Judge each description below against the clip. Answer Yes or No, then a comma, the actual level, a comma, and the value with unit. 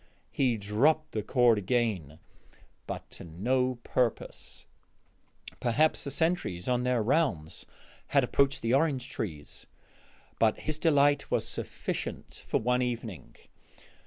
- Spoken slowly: Yes, slow, 120 wpm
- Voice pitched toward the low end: Yes, low, 125 Hz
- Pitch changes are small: No, average, 4.5 semitones